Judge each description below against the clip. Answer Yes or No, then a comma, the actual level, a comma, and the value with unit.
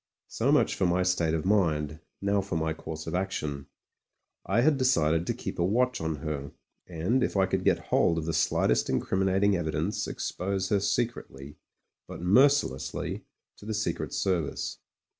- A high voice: No, very low, 90 Hz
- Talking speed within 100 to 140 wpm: No, average, 165 wpm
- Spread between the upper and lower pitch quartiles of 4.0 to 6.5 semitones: Yes, average, 4.3 semitones